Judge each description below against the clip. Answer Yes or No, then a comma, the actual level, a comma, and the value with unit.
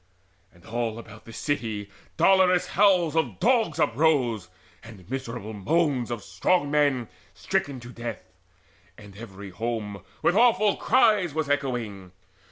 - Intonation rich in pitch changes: Yes, wide, 7.2 semitones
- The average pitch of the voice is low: Yes, low, 125 Hz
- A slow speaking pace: Yes, slow, 130 wpm